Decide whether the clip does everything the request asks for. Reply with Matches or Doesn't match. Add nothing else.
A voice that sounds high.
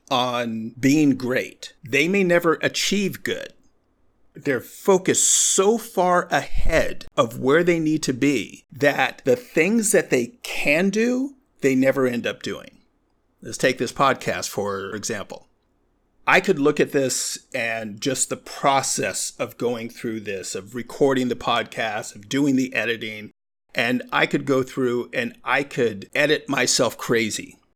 Doesn't match